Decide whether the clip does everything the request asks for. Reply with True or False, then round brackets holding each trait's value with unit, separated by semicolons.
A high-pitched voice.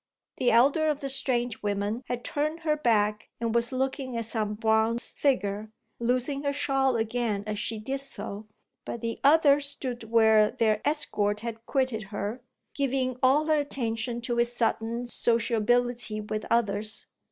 True (235 Hz)